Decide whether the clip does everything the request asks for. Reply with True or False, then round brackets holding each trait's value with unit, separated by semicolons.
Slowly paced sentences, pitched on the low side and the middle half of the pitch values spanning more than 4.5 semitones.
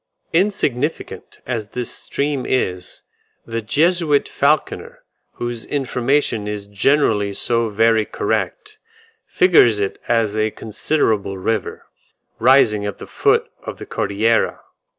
True (110 wpm; 115 Hz; 5.2 semitones)